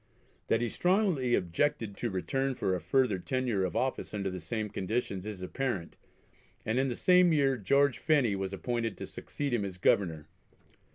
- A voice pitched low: Yes, low, 115 Hz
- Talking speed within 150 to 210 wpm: Yes, average, 175 wpm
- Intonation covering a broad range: Yes, wide, 5.7 semitones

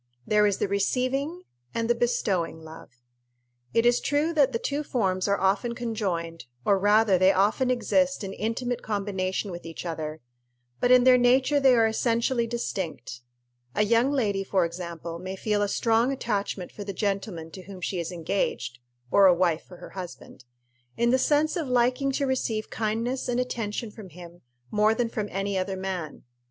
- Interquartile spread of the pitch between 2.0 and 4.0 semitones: No, average, 4.7 semitones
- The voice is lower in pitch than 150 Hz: No, high, 210 Hz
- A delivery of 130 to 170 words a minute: No, average, 180 wpm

